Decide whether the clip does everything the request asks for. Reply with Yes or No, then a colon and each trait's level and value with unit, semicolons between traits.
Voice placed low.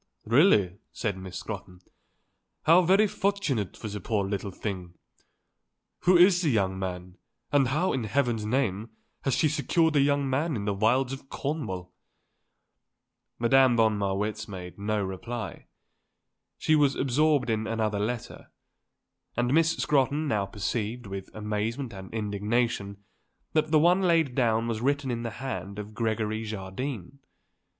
Yes: low, 115 Hz